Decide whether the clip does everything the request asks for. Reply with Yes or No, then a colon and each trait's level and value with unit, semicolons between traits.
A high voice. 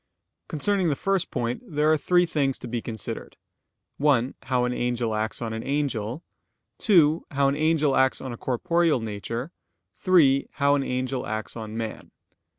No: low, 135 Hz